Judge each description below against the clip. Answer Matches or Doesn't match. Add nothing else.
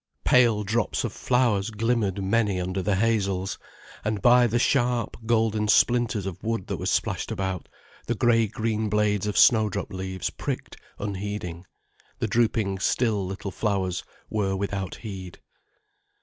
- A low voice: Matches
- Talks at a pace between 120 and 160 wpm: Matches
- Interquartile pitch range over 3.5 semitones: Doesn't match